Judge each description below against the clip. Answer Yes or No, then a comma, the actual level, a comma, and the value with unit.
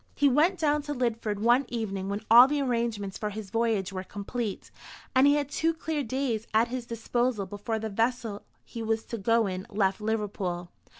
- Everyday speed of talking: Yes, average, 190 wpm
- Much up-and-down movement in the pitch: No, average, 3.7 semitones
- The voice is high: Yes, high, 230 Hz